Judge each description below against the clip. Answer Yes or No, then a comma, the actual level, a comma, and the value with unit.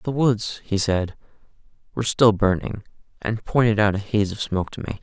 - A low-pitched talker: Yes, low, 105 Hz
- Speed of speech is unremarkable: Yes, average, 190 wpm